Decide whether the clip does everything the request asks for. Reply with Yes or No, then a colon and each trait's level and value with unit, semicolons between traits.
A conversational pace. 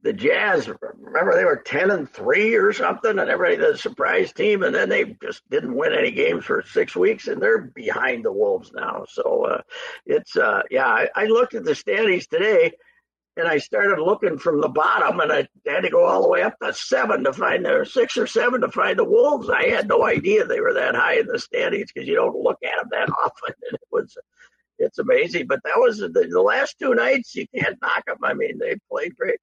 No: fast, 230 wpm